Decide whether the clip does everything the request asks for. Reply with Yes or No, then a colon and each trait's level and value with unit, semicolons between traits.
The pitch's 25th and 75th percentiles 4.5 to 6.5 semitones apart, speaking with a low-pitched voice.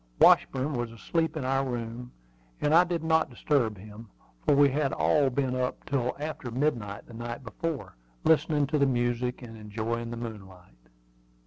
No: average, 3.9 semitones; low, 125 Hz